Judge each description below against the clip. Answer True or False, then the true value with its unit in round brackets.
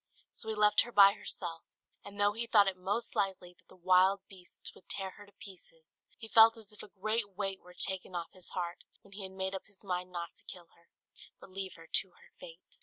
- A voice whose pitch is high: True (195 Hz)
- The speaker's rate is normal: False (240 wpm)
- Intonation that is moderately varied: False (2.2 semitones)